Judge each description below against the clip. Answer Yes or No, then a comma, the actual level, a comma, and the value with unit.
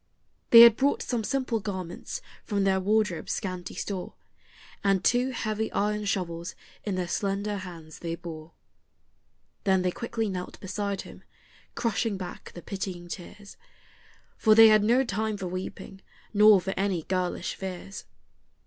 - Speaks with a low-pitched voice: No, high, 195 Hz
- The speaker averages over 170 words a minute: No, average, 145 wpm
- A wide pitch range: No, average, 2.9 semitones